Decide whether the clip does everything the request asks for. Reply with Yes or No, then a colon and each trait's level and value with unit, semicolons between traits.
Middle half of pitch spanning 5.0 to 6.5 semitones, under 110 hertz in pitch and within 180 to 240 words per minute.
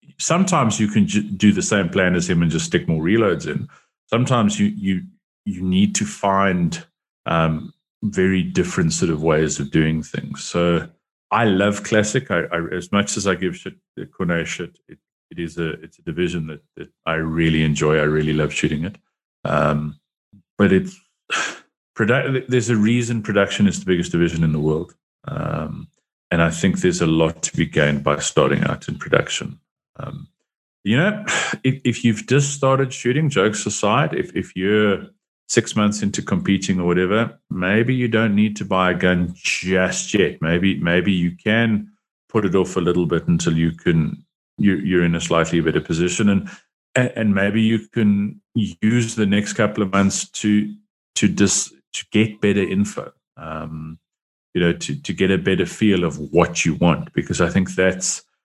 Yes: average, 5.3 semitones; low, 100 Hz; average, 185 wpm